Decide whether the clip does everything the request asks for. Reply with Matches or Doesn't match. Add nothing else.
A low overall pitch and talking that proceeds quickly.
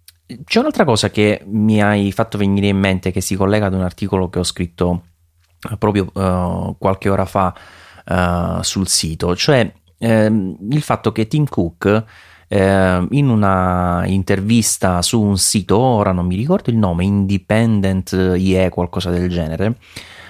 Doesn't match